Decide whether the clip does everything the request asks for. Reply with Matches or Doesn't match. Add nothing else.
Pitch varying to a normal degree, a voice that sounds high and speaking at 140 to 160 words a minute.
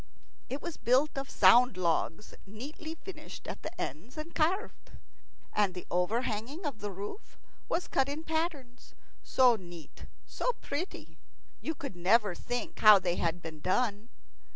Doesn't match